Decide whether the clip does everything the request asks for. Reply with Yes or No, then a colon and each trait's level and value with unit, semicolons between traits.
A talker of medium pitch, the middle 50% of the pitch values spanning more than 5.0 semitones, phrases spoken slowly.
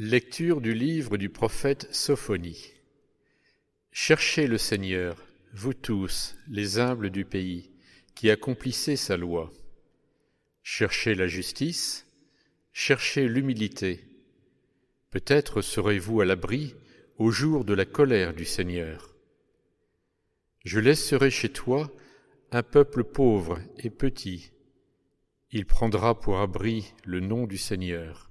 No: low, 110 Hz; wide, 5.6 semitones; slow, 110 wpm